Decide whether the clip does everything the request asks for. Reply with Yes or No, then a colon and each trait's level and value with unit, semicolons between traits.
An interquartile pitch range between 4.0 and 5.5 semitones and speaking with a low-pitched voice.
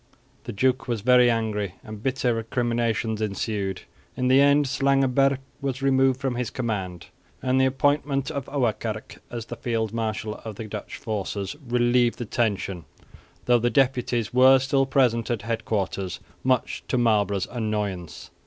No: average, 3.5 semitones; low, 120 Hz